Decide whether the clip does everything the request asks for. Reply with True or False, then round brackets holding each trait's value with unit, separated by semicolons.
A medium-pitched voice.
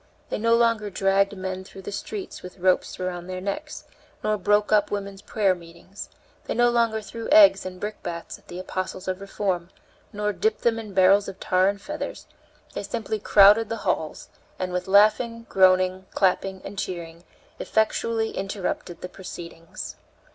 False (195 Hz)